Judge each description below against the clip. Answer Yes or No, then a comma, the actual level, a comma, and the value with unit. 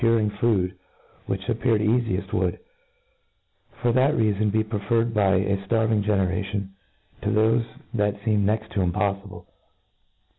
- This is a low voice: Yes, low, 105 Hz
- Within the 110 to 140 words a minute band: Yes, slow, 135 wpm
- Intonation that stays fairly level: Yes, narrow, 2.3 semitones